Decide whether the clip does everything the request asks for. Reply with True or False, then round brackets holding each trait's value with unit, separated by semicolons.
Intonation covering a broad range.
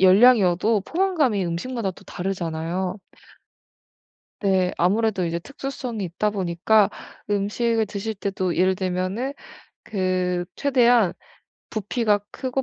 False (3.9 semitones)